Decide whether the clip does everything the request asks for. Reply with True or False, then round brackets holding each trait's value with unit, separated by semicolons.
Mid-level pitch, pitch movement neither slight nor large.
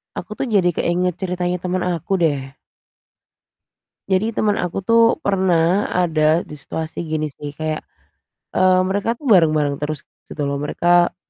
True (175 Hz; 3.2 semitones)